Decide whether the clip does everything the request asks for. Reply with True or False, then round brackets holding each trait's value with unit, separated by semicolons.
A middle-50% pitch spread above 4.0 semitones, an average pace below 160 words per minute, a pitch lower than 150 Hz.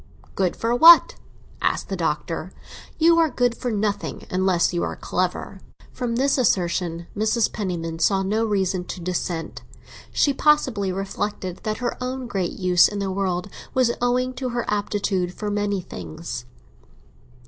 False (5.0 semitones; 150 wpm; 205 Hz)